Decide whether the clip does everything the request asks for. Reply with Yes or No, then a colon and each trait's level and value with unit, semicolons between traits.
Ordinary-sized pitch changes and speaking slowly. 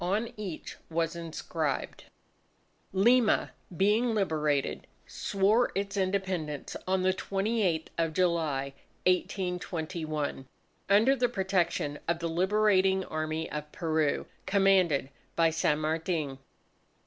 Yes: average, 3.9 semitones; slow, 100 wpm